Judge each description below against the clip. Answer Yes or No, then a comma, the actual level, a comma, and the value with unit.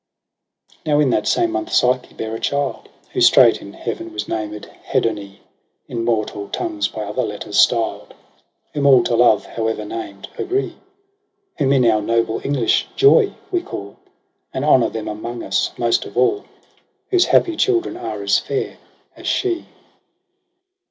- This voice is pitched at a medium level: No, low, 120 Hz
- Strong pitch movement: Yes, wide, 5.7 semitones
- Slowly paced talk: No, average, 160 wpm